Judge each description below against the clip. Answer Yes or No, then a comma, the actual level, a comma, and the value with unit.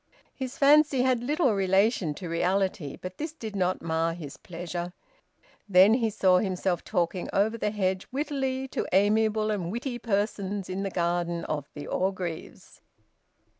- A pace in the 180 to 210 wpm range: No, average, 150 wpm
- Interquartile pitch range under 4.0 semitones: No, average, 4.5 semitones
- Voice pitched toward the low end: No, high, 195 Hz